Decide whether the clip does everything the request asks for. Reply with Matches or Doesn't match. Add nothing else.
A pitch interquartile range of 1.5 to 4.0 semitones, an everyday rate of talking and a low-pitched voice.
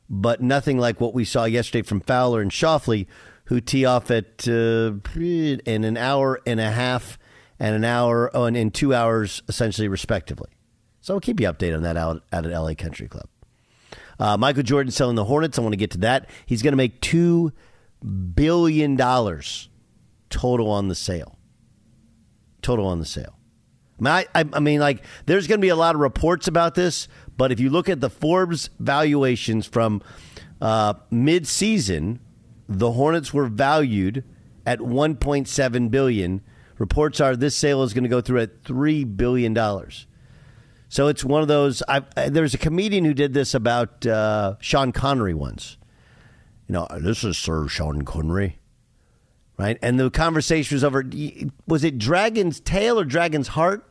Doesn't match